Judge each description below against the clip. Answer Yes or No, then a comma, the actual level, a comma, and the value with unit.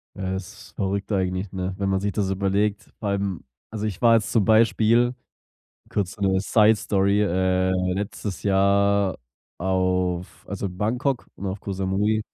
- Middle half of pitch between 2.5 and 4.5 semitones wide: No, narrow, 1.8 semitones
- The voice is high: No, low, 100 Hz